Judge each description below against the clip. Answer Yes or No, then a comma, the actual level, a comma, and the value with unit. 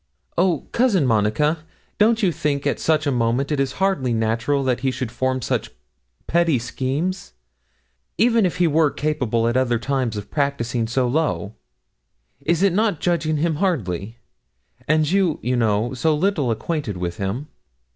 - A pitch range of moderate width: No, wide, 5.7 semitones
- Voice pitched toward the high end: No, medium, 140 Hz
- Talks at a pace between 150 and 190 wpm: Yes, average, 155 wpm